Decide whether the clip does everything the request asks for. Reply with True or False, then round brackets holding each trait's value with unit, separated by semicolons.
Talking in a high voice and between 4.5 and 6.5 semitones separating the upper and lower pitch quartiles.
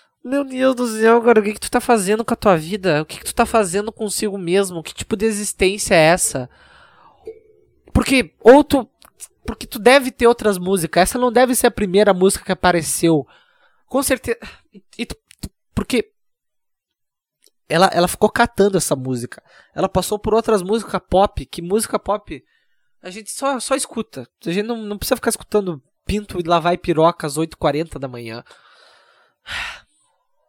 True (215 Hz; 5.2 semitones)